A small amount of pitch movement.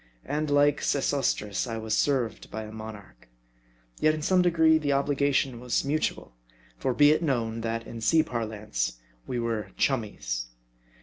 No: average, 4.9 semitones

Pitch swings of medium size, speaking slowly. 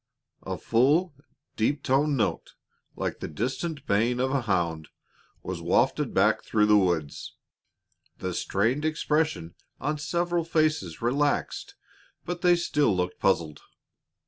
No: wide, 7.9 semitones; slow, 130 wpm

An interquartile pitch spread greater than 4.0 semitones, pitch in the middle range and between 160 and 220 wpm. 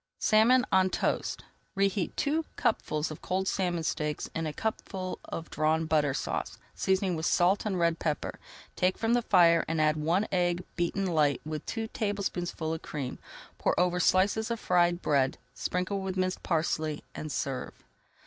No: average, 3.4 semitones; medium, 175 Hz; average, 165 wpm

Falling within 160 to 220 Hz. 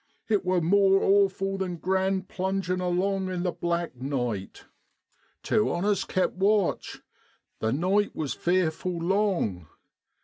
Yes: medium, 185 Hz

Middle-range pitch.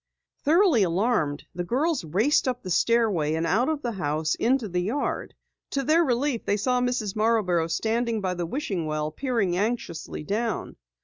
No: high, 220 Hz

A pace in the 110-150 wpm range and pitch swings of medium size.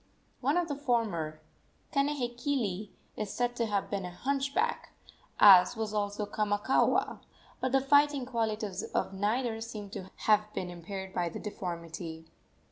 Yes: average, 140 wpm; average, 4.7 semitones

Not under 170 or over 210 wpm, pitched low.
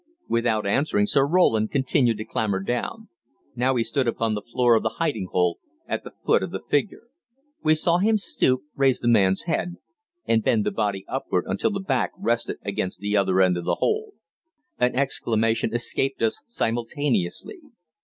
Yes: average, 175 wpm; low, 120 Hz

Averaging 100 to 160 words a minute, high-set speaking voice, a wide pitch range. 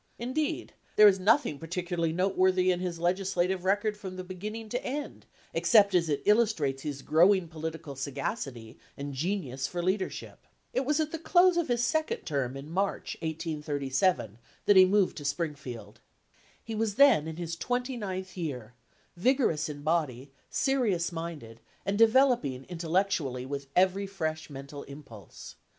No: average, 155 wpm; medium, 180 Hz; wide, 6.0 semitones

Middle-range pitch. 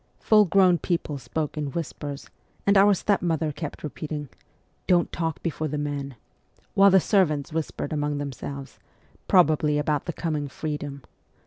Yes: medium, 155 Hz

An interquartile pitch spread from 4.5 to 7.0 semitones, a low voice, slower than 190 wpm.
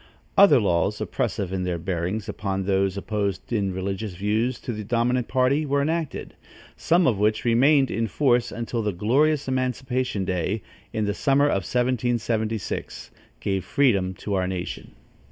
Yes: average, 4.8 semitones; low, 110 Hz; average, 155 wpm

